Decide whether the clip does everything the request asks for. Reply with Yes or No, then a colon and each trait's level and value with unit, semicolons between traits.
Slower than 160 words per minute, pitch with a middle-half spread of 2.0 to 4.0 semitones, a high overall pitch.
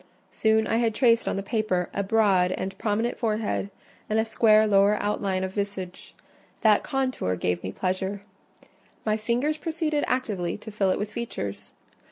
No: average, 165 wpm; average, 2.9 semitones; high, 210 Hz